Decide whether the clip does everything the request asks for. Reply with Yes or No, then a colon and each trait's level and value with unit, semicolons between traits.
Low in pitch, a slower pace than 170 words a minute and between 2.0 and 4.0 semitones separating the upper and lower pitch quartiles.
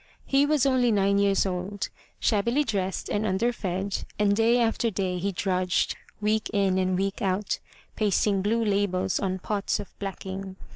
No: high, 200 Hz; average, 160 wpm; narrow, 2.4 semitones